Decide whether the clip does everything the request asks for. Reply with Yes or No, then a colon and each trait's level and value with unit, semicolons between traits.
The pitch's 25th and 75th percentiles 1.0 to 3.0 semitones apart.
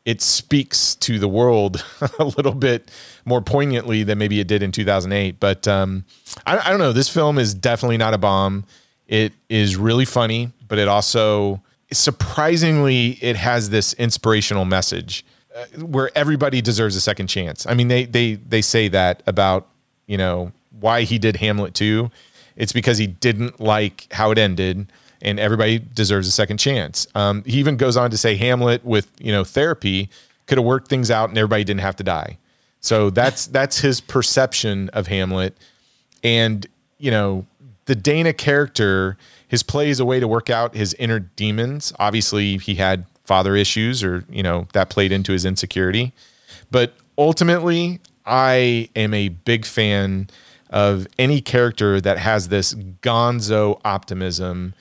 No: average, 3.9 semitones